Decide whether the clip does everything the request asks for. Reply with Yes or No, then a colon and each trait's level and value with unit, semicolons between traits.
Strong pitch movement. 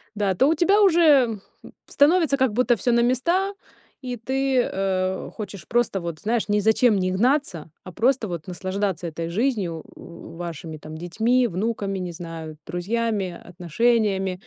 Yes: wide, 5.9 semitones